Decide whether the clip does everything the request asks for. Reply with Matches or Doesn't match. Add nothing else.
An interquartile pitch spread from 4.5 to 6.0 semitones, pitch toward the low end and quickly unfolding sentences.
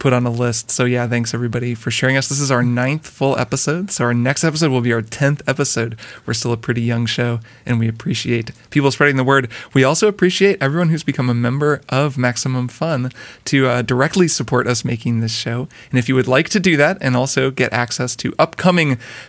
Doesn't match